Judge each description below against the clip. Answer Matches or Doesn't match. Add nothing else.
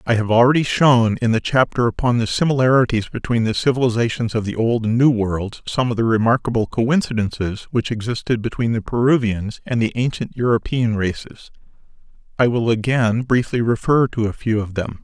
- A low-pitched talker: Matches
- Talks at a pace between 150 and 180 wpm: Matches